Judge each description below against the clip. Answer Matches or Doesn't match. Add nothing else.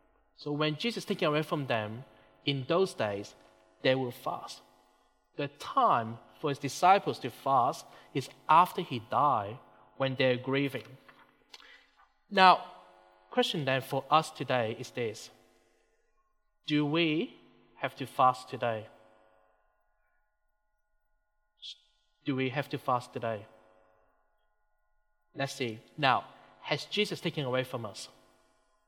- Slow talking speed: Matches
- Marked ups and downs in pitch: Matches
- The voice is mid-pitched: Matches